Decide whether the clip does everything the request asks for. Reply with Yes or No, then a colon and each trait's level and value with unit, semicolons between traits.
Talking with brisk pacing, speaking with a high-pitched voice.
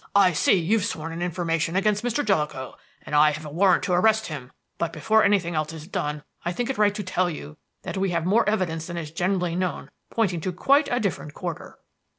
No: fast, 220 wpm; medium, 180 Hz